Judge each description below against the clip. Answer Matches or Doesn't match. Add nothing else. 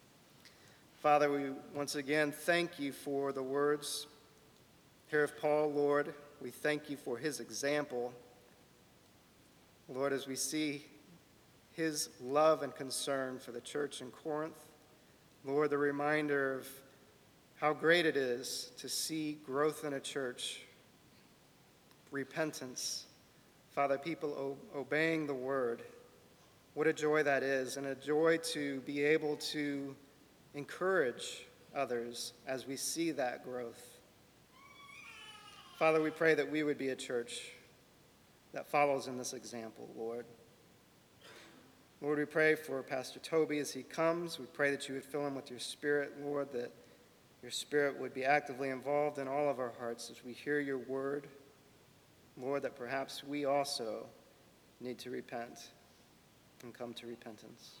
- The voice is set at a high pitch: Doesn't match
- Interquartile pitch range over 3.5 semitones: Doesn't match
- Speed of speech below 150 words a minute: Matches